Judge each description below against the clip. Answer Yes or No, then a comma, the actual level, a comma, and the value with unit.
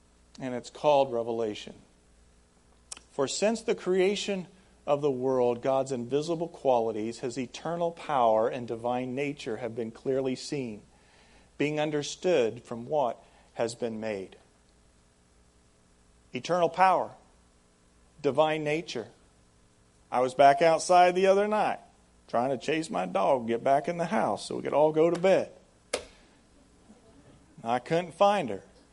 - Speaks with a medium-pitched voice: No, low, 125 Hz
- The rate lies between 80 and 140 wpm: Yes, slow, 135 wpm